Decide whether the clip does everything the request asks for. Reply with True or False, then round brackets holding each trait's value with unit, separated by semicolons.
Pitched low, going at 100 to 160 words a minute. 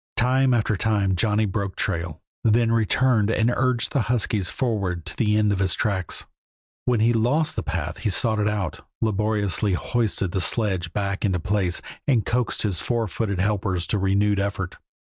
False (105 Hz; 175 wpm)